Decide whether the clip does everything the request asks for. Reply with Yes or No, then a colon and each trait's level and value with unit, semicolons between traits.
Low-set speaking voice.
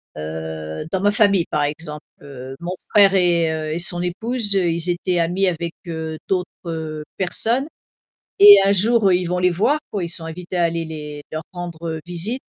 No: medium, 175 Hz